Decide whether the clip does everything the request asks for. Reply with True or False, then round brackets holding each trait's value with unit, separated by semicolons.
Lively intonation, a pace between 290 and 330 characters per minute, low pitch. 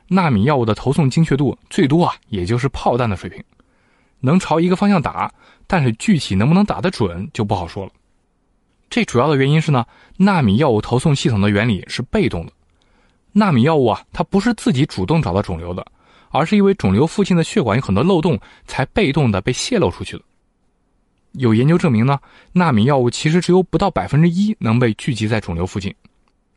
False (8.0 semitones; 310 characters per minute; 145 Hz)